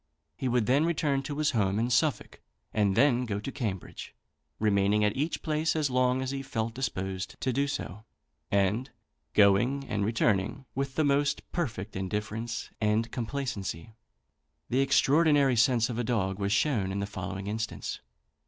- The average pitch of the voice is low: Yes, low, 115 Hz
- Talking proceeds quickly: No, average, 160 wpm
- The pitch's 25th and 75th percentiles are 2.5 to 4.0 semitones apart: No, average, 5.1 semitones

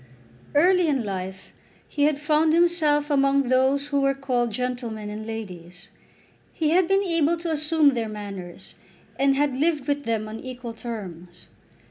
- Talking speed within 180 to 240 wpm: No, average, 155 wpm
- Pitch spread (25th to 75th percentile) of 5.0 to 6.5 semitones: Yes, wide, 5.5 semitones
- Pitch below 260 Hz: No, very high, 275 Hz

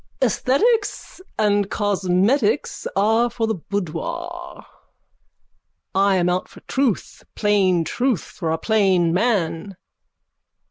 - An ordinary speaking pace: No, slow, 105 wpm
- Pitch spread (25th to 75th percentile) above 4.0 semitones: Yes, average, 5.1 semitones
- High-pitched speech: Yes, high, 205 Hz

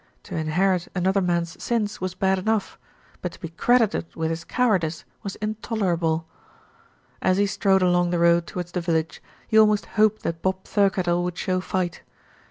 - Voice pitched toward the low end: No, medium, 185 Hz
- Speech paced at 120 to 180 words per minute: Yes, average, 170 wpm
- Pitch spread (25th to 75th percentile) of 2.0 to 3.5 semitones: Yes, average, 2.9 semitones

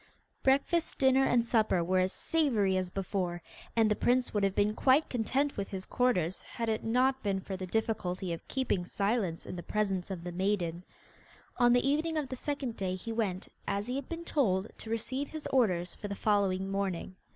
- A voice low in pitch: No, high, 210 Hz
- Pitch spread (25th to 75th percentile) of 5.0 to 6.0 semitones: Yes, wide, 5.4 semitones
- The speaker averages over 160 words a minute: Yes, average, 200 wpm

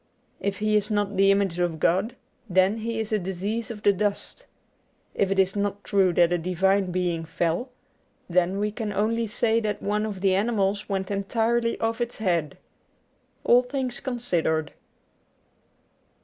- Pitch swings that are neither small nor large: Yes, average, 3.1 semitones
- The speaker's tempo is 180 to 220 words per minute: No, average, 165 wpm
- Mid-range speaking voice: No, high, 200 Hz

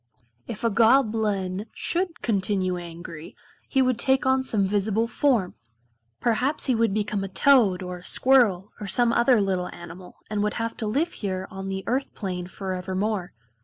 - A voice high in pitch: Yes, high, 210 Hz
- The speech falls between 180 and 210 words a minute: No, average, 165 wpm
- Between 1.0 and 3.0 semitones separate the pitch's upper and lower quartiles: No, average, 4.2 semitones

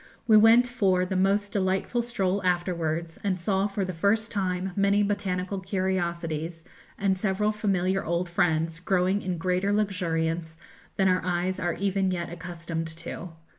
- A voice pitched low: No, medium, 185 Hz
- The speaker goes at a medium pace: Yes, average, 150 wpm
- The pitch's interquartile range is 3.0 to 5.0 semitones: No, narrow, 2.4 semitones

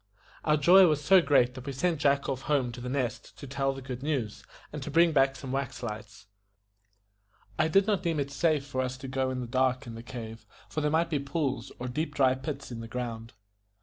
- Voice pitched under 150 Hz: Yes, low, 135 Hz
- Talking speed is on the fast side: Yes, fast, 235 wpm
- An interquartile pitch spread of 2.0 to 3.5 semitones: Yes, average, 3.1 semitones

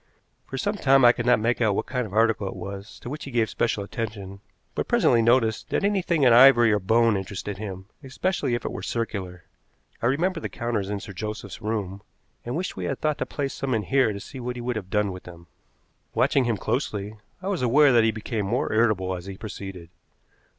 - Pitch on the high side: No, low, 115 Hz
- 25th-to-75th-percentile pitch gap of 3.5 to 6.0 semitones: Yes, average, 4.1 semitones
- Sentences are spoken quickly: Yes, fast, 225 wpm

